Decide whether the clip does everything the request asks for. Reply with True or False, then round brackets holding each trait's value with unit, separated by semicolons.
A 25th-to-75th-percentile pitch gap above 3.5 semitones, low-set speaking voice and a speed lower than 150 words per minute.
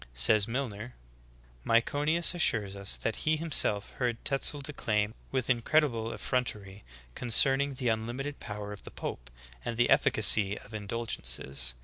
True (4.7 semitones; 115 Hz; 135 wpm)